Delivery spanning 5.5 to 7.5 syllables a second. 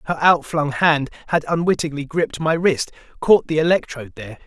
Yes: 5.7 syllables/s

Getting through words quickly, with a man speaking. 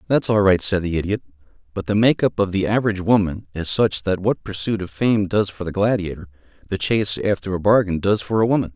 Yes: fast, 225 wpm; male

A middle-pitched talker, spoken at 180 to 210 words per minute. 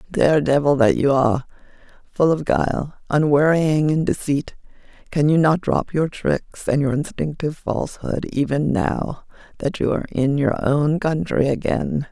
No: medium, 145 Hz; average, 155 wpm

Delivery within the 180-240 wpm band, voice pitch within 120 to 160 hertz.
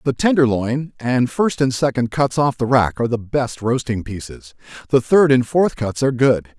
Yes: average, 200 wpm; low, 130 Hz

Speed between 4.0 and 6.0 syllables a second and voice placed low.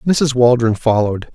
Yes: 5.2 syllables/s; low, 125 Hz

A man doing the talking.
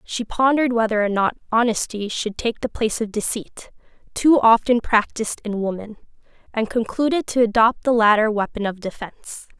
No: female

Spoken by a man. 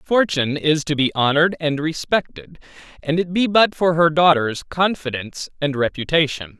Yes: male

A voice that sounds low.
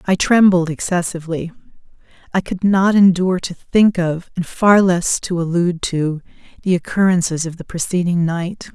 No: medium, 180 Hz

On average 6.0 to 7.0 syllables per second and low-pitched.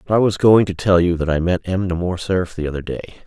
Yes: 6.1 syllables/s; very low, 90 Hz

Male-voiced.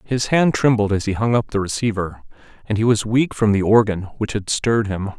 Yes: male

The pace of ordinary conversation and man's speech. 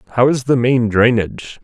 Yes: average, 185 wpm; male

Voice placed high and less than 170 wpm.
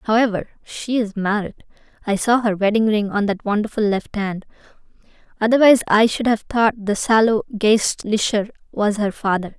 Yes: high, 215 Hz; average, 155 wpm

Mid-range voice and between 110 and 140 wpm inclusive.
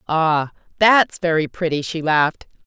Yes: medium, 165 Hz; slow, 135 wpm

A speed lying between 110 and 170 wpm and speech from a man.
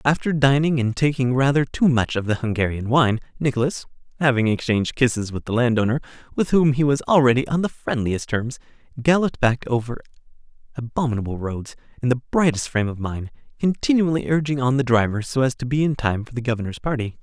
No: average, 180 wpm; male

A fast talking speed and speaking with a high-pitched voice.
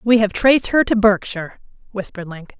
No: average, 185 wpm; high, 210 Hz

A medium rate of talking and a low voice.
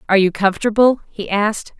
No: average, 165 wpm; high, 205 Hz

